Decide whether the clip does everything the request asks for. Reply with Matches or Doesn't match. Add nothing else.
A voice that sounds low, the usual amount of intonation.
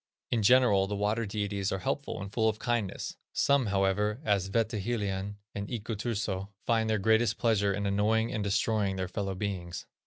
Doesn't match